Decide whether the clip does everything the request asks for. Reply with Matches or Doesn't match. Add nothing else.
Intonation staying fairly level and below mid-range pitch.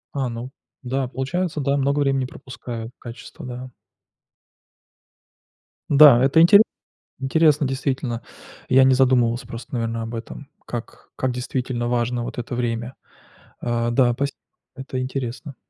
Matches